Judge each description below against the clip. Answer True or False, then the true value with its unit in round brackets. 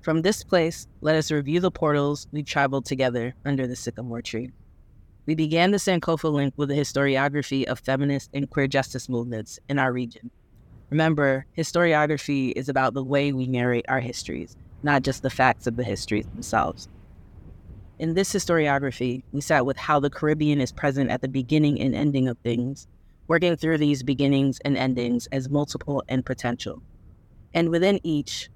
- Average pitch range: True (3.5 semitones)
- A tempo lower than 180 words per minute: True (170 wpm)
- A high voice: False (135 Hz)